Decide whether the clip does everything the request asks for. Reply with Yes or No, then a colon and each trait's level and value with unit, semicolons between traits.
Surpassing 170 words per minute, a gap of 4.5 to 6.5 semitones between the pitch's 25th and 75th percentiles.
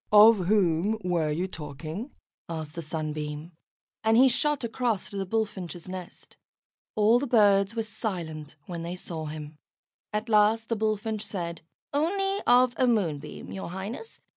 No: average, 150 wpm; average, 5.2 semitones